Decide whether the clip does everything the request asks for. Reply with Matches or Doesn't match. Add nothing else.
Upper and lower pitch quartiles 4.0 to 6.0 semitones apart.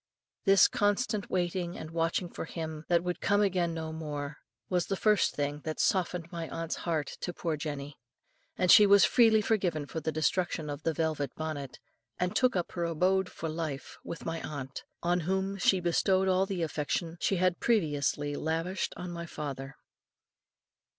Doesn't match